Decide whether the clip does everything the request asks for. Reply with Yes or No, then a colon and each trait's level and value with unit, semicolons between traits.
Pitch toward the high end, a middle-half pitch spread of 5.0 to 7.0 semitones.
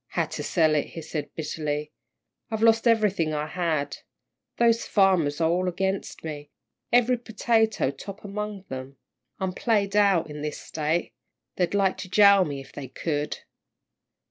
No: medium, 180 Hz; wide, 5.4 semitones